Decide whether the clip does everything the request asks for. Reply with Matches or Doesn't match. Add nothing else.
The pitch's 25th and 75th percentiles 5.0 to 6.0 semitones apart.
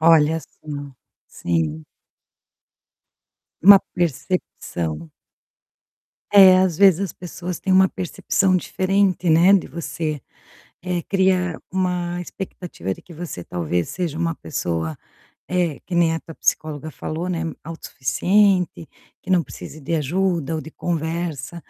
Doesn't match